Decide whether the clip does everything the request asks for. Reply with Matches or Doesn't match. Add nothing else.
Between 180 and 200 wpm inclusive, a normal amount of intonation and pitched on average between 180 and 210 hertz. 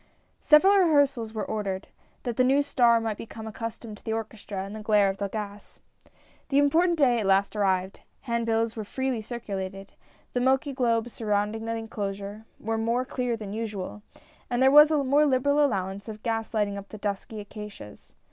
Doesn't match